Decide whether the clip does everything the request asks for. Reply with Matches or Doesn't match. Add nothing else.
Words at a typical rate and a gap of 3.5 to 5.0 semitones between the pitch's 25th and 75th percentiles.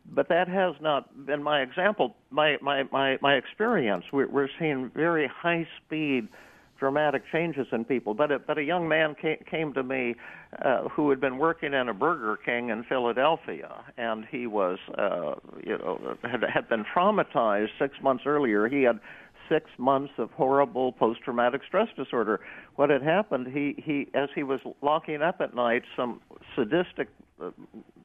Doesn't match